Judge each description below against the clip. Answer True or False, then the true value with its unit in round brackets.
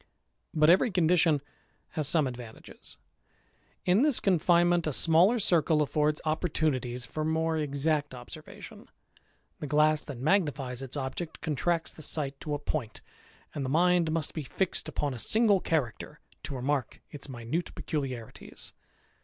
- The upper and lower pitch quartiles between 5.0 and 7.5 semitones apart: False (3.5 semitones)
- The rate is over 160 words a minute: False (145 wpm)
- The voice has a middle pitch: True (155 Hz)